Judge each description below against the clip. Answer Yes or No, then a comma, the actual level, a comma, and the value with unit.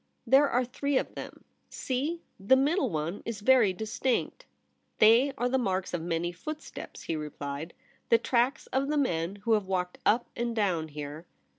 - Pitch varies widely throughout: Yes, wide, 7.1 semitones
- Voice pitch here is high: Yes, high, 225 Hz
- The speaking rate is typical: Yes, average, 185 wpm